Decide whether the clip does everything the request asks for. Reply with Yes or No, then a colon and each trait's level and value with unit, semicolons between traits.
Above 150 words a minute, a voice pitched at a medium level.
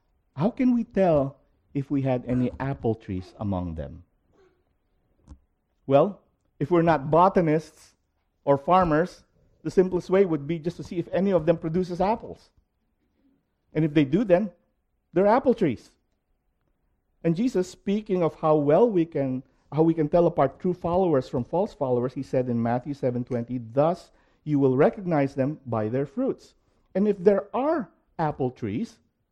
Yes: average, 160 wpm; medium, 155 Hz